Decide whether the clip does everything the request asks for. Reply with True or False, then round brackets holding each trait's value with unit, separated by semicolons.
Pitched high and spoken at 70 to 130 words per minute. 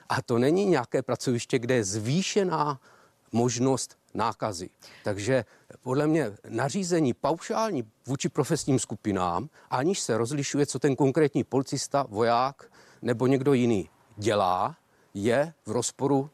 False (135 Hz; 120 wpm)